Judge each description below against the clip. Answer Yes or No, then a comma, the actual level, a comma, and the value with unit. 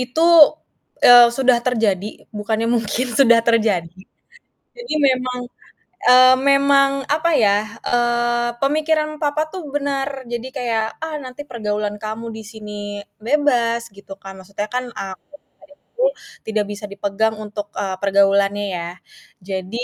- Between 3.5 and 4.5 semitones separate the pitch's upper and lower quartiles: Yes, average, 4.1 semitones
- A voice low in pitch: No, high, 235 Hz